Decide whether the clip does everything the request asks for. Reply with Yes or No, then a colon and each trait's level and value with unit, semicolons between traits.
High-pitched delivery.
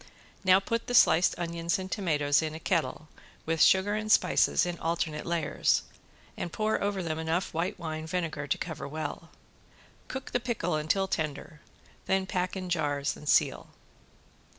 No: medium, 170 Hz